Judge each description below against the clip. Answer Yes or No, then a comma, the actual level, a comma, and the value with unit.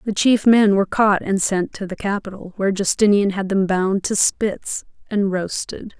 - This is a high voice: Yes, high, 200 Hz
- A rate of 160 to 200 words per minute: Yes, average, 190 wpm